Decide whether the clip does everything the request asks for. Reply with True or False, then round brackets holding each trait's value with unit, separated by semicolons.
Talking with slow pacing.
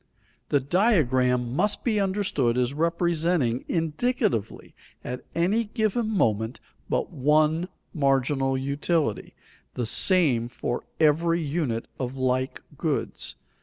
True (105 wpm)